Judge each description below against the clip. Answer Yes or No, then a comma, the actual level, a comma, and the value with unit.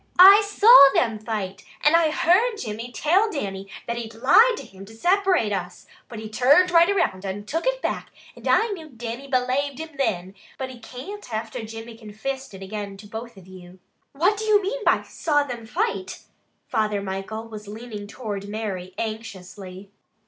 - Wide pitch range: Yes, wide, 7.6 semitones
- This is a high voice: Yes, high, 230 Hz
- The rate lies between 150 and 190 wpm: Yes, average, 180 wpm